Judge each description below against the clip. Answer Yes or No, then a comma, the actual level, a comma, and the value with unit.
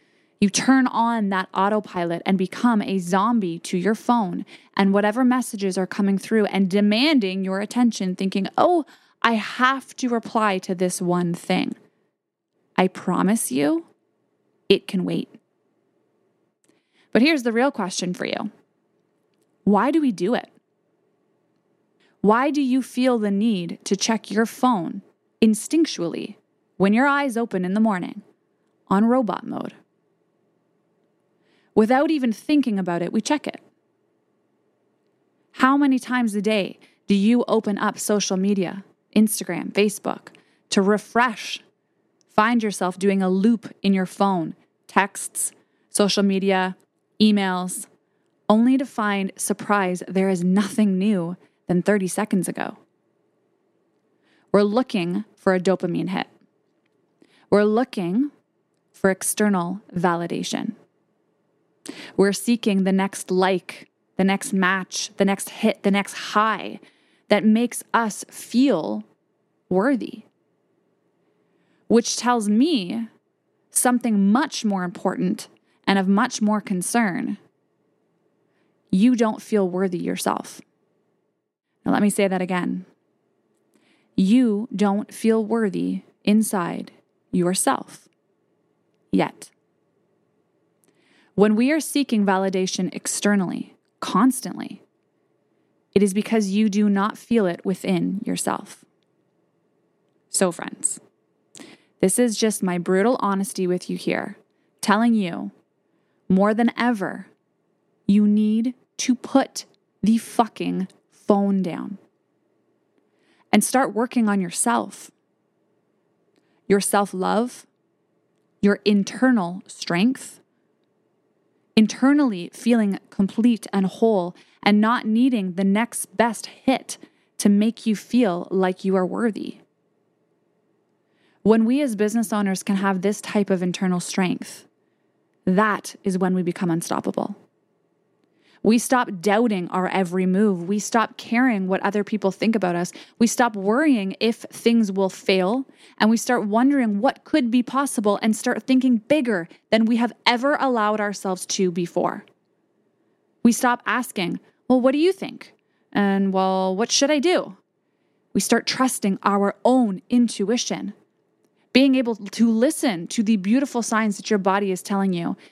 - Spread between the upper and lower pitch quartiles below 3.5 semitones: No, average, 3.8 semitones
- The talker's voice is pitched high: Yes, high, 210 Hz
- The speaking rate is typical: No, slow, 125 wpm